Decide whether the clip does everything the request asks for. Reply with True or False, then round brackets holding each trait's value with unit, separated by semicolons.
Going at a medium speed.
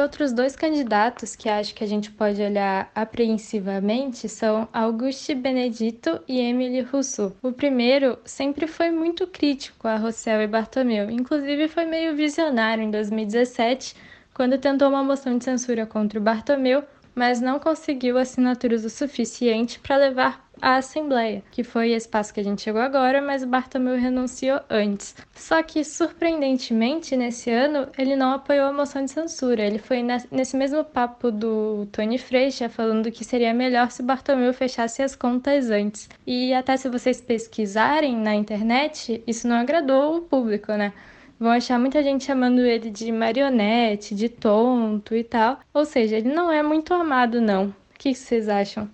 True (165 wpm)